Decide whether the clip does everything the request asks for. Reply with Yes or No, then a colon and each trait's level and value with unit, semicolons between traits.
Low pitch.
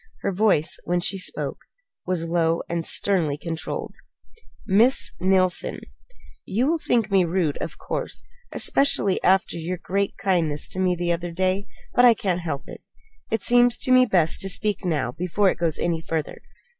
No: medium, 185 Hz